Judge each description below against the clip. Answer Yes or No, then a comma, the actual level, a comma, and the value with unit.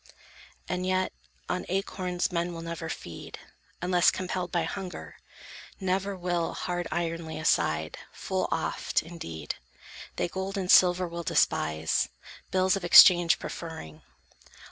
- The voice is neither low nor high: Yes, medium, 175 Hz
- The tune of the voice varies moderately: No, narrow, 2.0 semitones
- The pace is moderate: No, slow, 125 wpm